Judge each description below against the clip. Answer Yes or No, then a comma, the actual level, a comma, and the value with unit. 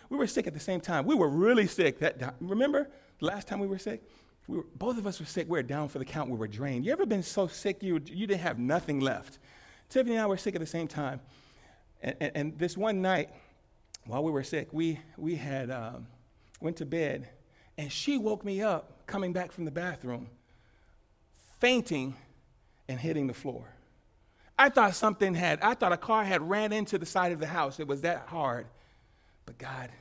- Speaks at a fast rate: Yes, fast, 220 wpm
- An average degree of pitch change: No, wide, 6.8 semitones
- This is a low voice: No, medium, 160 Hz